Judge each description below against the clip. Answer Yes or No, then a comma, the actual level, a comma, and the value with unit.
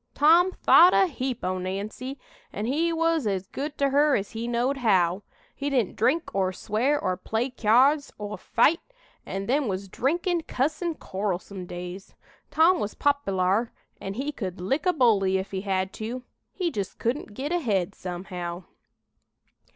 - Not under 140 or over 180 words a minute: Yes, average, 160 wpm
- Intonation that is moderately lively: No, wide, 6.9 semitones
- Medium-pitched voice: No, high, 230 Hz